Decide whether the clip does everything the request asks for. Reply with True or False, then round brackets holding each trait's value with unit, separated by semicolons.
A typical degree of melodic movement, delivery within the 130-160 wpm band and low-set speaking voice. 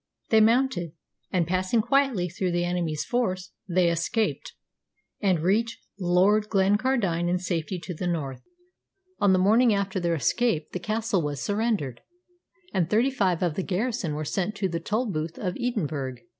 False (4.2 semitones; 155 wpm; 185 Hz)